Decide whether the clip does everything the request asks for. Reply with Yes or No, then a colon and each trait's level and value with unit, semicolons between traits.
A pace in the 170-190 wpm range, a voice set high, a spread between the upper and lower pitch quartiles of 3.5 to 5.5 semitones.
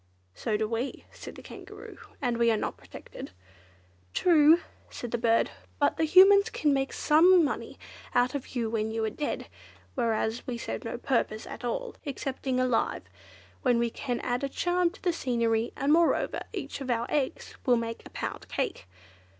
Yes: average, 175 wpm; very high, 250 Hz; average, 4.6 semitones